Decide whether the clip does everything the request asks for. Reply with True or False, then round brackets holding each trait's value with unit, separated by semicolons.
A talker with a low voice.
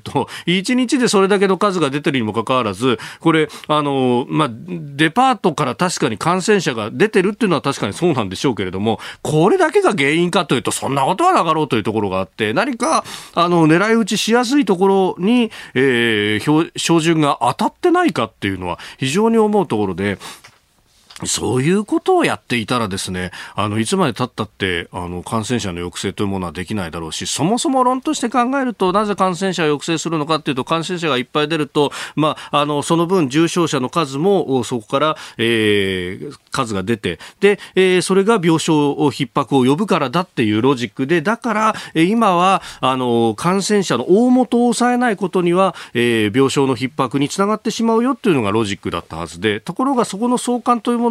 False (155 Hz)